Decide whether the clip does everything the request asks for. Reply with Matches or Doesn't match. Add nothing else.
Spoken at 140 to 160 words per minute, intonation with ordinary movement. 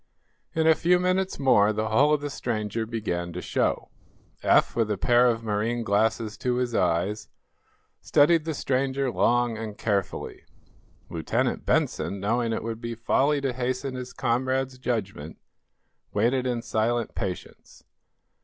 Matches